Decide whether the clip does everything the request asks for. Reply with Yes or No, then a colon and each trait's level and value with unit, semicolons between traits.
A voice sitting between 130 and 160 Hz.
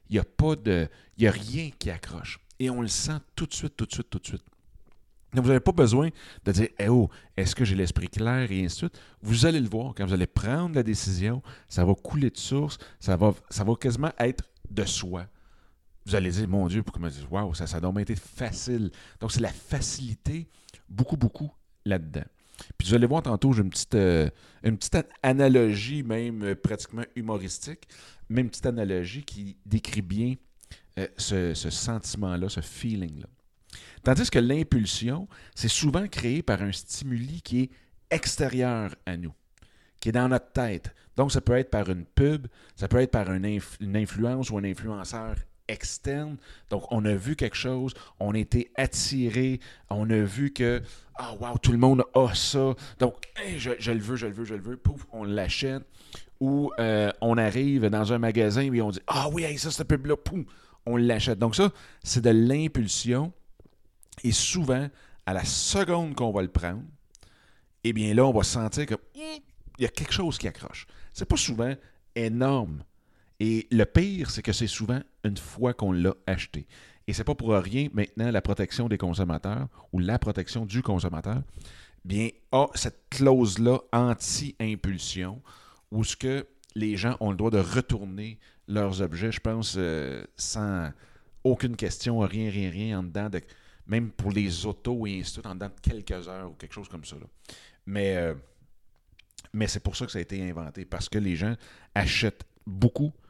No: low, 110 Hz